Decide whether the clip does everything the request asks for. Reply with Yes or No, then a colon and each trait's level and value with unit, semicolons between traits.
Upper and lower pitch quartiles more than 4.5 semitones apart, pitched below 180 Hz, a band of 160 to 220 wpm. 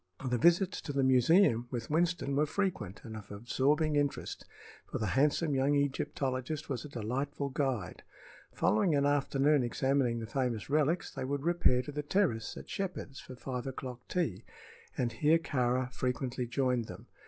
No: average, 3.2 semitones; low, 135 Hz; average, 165 wpm